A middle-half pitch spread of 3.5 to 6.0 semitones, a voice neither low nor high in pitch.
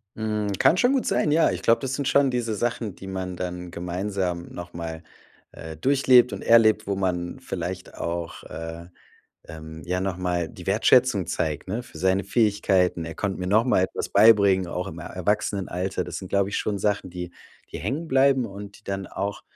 No: average, 3.9 semitones; very low, 95 Hz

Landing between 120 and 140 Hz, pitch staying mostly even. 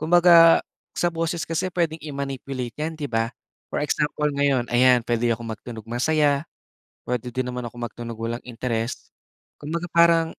No: low, 135 Hz; average, 5.2 semitones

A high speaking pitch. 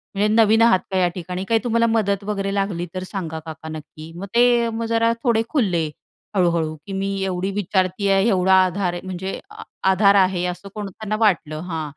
Yes: high, 195 Hz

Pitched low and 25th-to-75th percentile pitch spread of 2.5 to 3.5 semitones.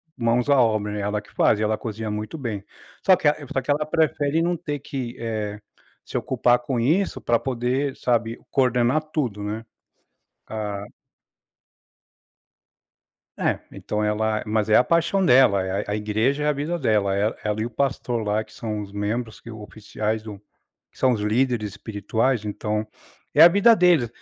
No: low, 115 Hz; average, 4.1 semitones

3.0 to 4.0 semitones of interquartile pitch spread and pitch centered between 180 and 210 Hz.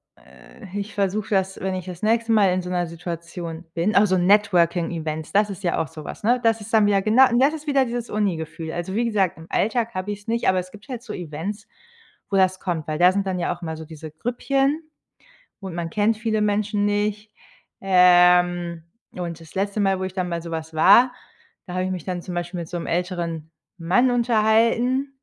Yes: average, 3.7 semitones; high, 190 Hz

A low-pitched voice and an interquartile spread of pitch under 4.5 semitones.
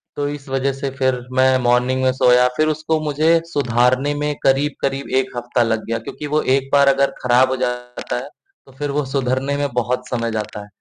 Yes: low, 130 Hz; narrow, 2.4 semitones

